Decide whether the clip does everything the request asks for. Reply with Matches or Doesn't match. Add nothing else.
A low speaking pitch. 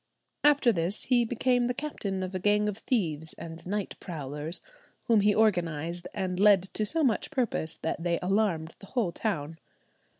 Doesn't match